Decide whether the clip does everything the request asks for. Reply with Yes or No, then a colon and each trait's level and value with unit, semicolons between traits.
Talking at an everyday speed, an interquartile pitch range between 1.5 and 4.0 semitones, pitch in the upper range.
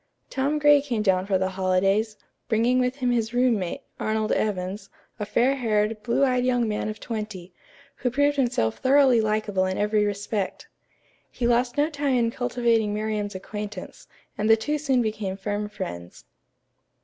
Yes: average, 160 wpm; average, 3.4 semitones; high, 220 Hz